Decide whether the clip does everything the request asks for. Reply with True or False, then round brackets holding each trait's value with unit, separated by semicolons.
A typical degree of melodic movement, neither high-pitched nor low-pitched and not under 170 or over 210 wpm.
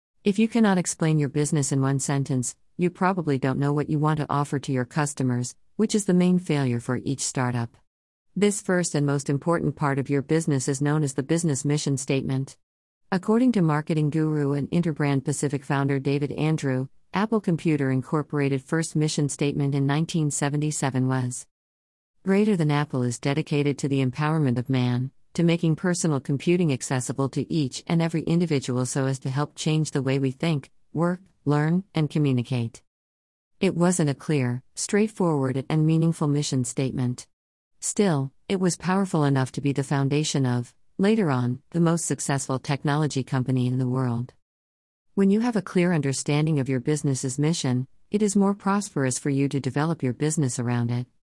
True (3.6 semitones; 145 Hz; 175 wpm)